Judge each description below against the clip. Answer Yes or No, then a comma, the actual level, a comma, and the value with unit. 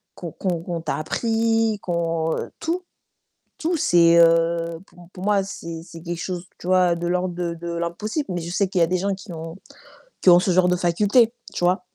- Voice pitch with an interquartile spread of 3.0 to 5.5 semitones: No, narrow, 2.4 semitones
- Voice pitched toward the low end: No, medium, 175 Hz